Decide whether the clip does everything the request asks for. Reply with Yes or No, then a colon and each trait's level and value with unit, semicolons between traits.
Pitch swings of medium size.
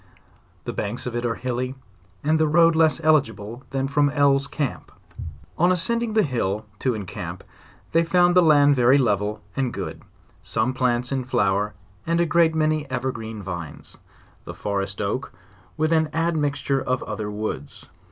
No: wide, 5.9 semitones